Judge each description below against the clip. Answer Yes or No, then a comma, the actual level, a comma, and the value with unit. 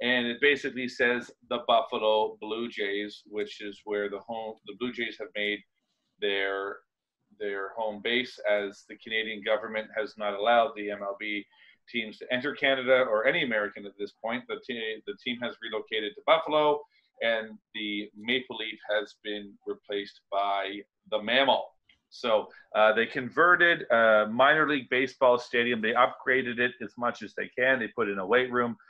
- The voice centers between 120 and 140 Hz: No, low, 110 Hz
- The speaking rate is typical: Yes, average, 170 wpm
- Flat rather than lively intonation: No, average, 3.4 semitones